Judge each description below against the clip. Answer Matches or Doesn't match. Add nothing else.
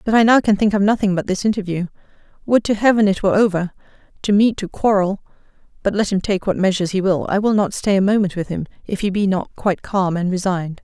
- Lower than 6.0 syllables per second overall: Doesn't match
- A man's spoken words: Doesn't match